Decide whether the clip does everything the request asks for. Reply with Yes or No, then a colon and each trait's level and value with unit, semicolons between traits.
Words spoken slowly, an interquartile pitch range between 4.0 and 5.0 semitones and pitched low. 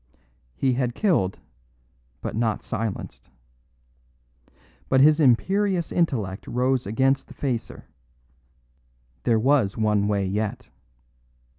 Yes: slow, 100 wpm; average, 4.3 semitones; low, 125 Hz